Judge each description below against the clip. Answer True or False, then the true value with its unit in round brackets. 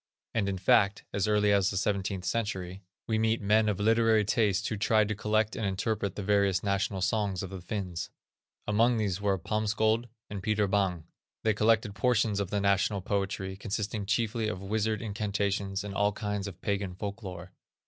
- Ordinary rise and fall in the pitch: False (1.8 semitones)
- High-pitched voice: False (100 Hz)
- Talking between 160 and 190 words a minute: True (180 wpm)